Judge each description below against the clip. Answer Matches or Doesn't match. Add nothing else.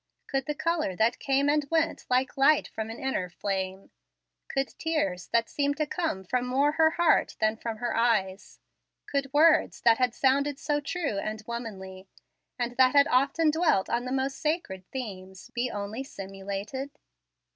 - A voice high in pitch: Matches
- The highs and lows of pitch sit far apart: Matches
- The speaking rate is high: Doesn't match